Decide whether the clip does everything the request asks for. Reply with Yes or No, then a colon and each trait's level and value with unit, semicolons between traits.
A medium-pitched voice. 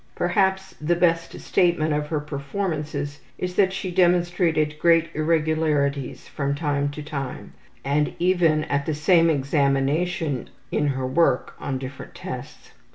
Yes: medium, 155 Hz